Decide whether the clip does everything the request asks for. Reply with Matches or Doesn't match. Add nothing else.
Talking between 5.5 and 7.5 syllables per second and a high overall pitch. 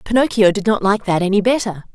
Matches